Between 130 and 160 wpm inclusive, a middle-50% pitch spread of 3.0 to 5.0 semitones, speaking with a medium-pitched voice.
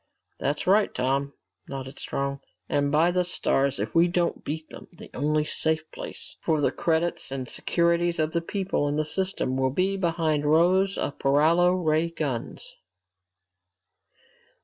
Yes: average, 155 wpm; average, 3.4 semitones; medium, 160 Hz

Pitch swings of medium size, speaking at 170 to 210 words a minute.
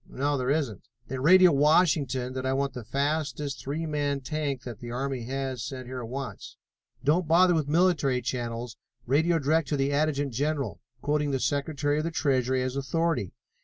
Yes: average, 3.0 semitones; average, 180 wpm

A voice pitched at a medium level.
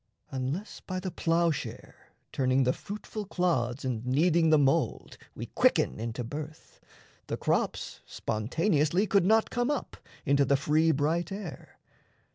Yes: medium, 155 Hz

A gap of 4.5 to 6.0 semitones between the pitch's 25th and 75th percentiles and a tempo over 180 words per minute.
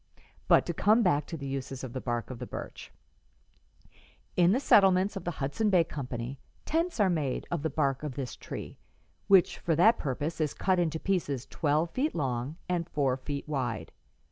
Yes: average, 5.1 semitones; average, 190 wpm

